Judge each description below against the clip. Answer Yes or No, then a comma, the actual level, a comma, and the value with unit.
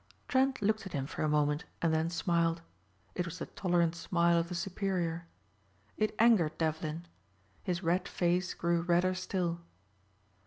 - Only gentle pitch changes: Yes, narrow, 1.8 semitones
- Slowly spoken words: No, average, 155 wpm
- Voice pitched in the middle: Yes, medium, 170 Hz